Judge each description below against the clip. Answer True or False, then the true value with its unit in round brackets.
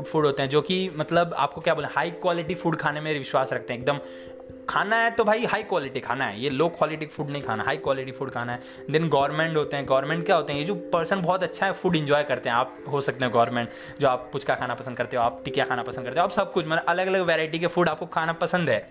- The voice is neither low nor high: True (155 Hz)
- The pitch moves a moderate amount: True (4.8 semitones)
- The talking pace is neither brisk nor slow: False (270 wpm)